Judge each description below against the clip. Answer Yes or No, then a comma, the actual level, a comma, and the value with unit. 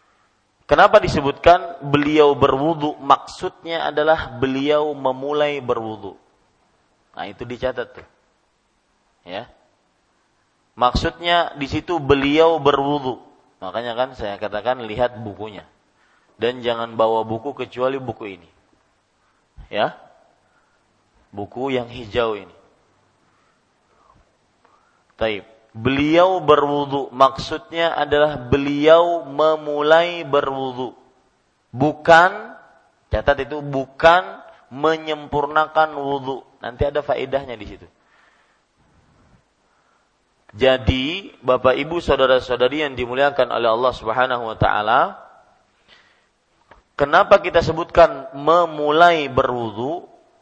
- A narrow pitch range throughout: No, average, 4.1 semitones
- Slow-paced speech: Yes, slow, 85 wpm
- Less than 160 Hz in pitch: Yes, medium, 140 Hz